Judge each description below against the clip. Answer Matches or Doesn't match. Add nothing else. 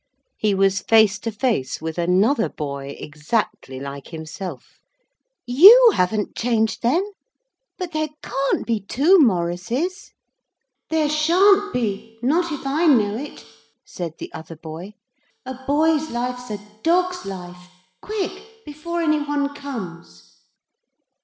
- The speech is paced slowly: Matches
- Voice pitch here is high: Matches